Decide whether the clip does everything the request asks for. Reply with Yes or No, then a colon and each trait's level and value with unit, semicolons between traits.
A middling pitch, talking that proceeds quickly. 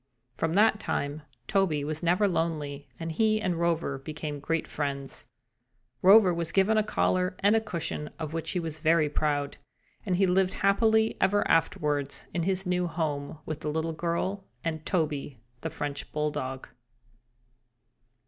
No: medium, 165 Hz; average, 155 wpm